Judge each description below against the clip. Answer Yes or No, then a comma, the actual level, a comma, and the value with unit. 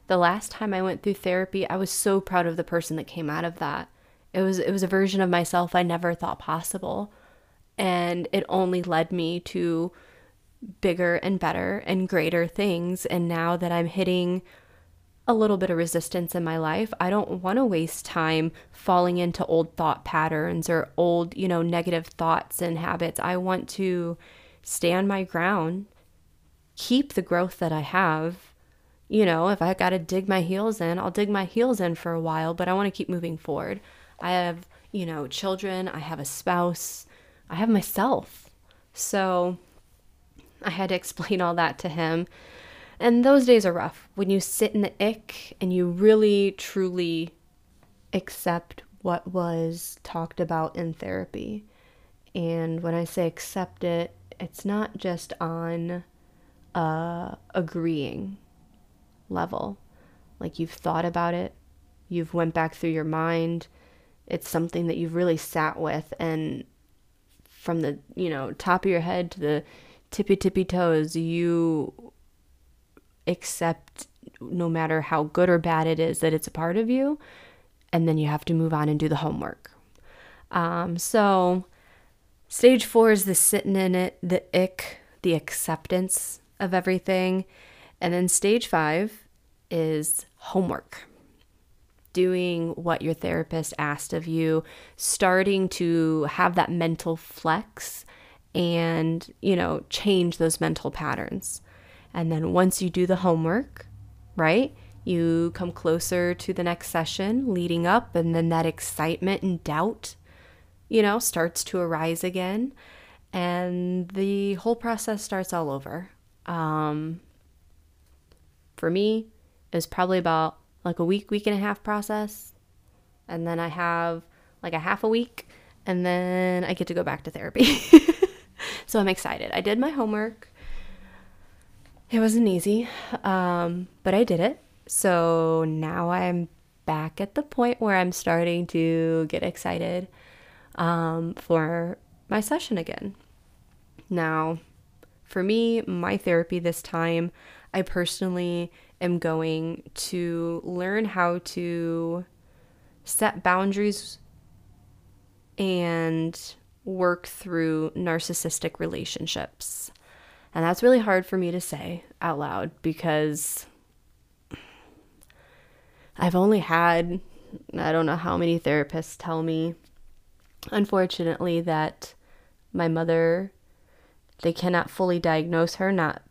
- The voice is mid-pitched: Yes, medium, 170 Hz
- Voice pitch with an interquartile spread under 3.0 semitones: Yes, narrow, 2.5 semitones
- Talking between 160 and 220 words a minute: No, average, 145 wpm